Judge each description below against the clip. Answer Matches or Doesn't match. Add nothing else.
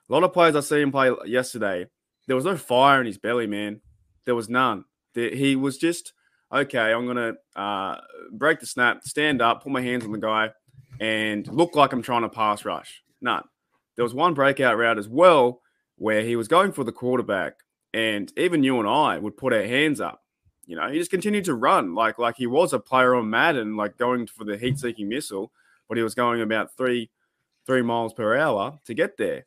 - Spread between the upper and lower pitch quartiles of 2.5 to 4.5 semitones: Matches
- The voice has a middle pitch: Doesn't match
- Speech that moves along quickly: Matches